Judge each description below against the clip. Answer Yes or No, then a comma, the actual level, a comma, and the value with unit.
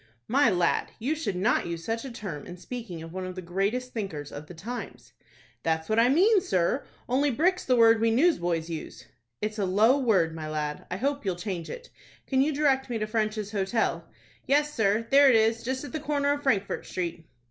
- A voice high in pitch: Yes, high, 220 Hz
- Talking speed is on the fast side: Yes, fast, 215 wpm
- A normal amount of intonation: No, wide, 6.8 semitones